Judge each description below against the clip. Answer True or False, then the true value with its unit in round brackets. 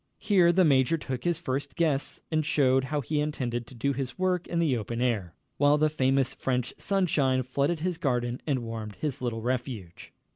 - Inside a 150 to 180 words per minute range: False (190 wpm)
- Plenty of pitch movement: False (3.9 semitones)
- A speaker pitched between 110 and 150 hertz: True (135 Hz)